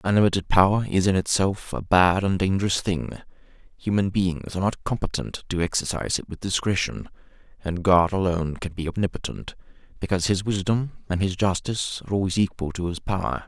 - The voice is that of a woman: No, male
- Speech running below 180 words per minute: Yes, average, 170 wpm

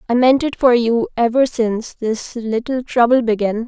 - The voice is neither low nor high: No, high, 240 Hz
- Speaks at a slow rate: No, average, 180 wpm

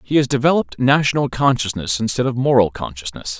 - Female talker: No, male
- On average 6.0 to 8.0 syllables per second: Yes, 6.1 syllables/s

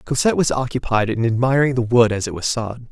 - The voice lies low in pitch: Yes, low, 120 Hz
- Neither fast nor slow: No, fast, 225 wpm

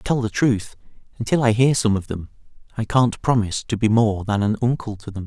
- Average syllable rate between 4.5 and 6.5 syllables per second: Yes, 5.8 syllables/s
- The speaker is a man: Yes, male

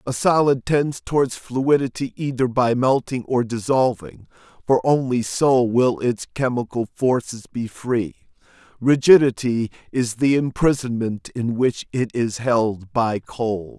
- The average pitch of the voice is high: No, low, 125 Hz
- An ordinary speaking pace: No, slow, 130 wpm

